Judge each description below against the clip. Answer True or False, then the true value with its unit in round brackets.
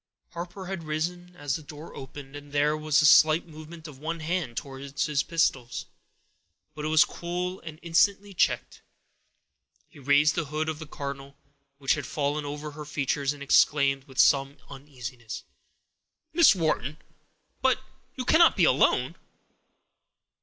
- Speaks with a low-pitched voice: False (150 Hz)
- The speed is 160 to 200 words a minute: False (150 wpm)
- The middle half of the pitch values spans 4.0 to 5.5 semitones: False (2.9 semitones)